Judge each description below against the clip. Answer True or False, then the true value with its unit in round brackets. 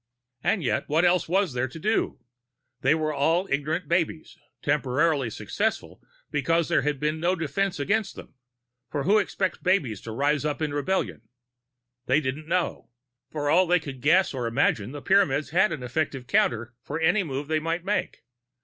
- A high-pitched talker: False (155 Hz)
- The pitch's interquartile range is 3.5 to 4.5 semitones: True (4.2 semitones)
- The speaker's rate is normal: True (175 wpm)